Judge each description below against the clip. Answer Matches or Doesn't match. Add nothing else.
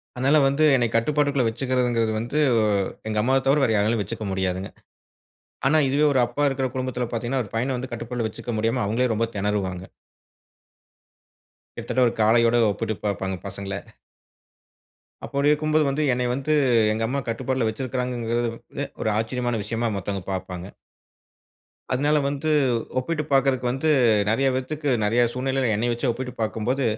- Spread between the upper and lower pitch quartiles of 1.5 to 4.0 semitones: Matches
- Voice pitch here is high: Doesn't match